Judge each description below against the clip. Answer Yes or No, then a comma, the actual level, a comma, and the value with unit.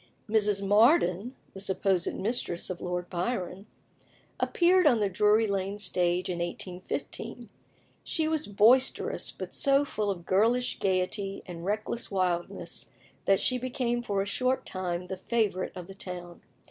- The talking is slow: No, average, 145 wpm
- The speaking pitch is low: No, high, 195 Hz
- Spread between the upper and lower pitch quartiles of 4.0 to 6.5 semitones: Yes, average, 4.5 semitones